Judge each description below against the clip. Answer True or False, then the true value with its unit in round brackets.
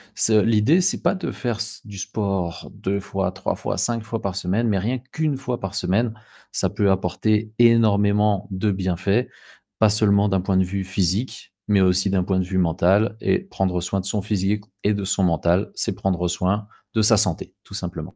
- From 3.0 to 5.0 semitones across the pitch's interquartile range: False (2.5 semitones)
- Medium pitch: False (100 Hz)